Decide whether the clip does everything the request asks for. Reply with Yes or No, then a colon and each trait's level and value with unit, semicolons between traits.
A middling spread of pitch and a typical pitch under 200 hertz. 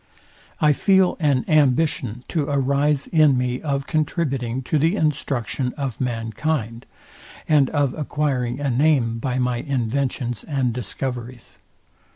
Yes: average, 3.3 semitones; low, 135 Hz